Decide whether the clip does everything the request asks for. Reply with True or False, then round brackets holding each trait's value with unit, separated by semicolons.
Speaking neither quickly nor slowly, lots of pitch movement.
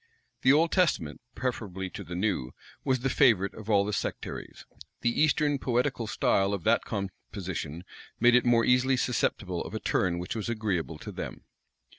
False (170 wpm; 4.9 semitones)